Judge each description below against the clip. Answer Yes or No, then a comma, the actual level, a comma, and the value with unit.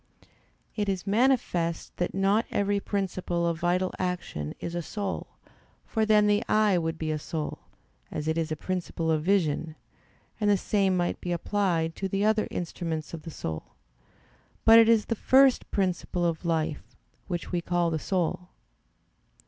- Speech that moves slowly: No, average, 165 wpm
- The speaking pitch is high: No, medium, 180 Hz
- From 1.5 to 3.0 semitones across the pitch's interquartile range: No, average, 3.7 semitones